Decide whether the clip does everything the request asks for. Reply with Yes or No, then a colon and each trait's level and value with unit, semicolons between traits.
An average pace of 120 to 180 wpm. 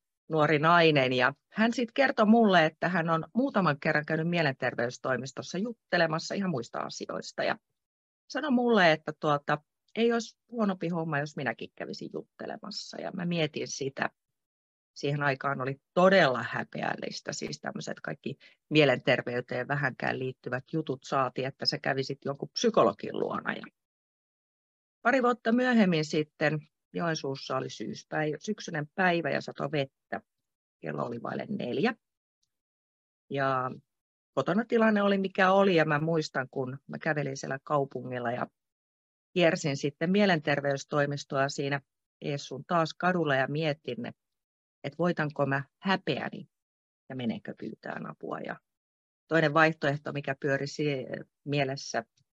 Yes: average, 125 wpm